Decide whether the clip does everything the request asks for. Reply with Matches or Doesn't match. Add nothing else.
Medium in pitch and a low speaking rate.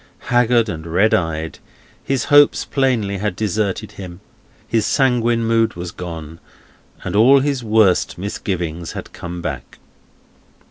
Doesn't match